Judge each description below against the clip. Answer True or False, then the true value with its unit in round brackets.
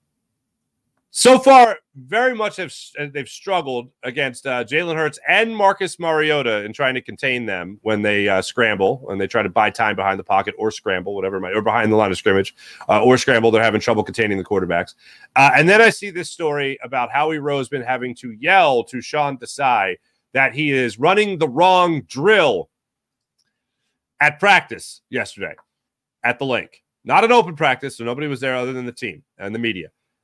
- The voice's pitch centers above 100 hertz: True (135 Hz)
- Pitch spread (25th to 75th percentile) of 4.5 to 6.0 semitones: True (5.6 semitones)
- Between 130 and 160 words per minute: False (190 wpm)